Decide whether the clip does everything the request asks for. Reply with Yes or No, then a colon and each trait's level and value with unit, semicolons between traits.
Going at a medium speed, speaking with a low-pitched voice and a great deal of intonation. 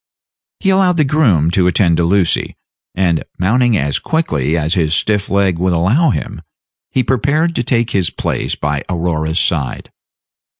Yes: average, 160 wpm; very low, 95 Hz; wide, 7.1 semitones